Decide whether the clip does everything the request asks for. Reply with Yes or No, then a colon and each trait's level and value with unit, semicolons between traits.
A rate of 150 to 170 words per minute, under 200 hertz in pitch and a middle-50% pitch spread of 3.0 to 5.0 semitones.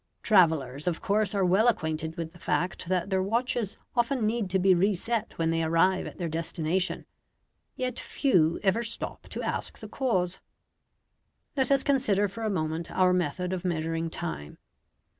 Yes: average, 165 wpm; medium, 185 Hz; average, 4.7 semitones